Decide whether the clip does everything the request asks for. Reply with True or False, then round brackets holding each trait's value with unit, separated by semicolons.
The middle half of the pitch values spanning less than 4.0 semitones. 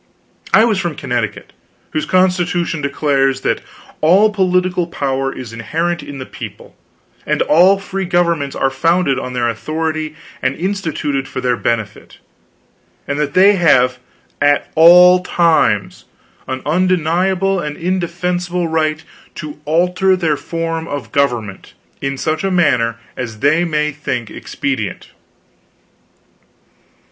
False (4.7 semitones)